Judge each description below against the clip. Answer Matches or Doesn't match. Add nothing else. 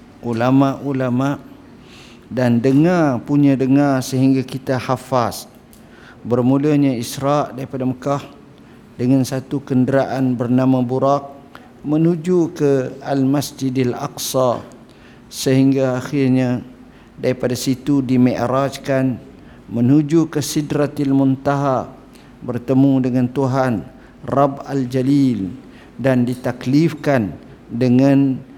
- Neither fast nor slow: Doesn't match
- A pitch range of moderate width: Doesn't match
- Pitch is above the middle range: Doesn't match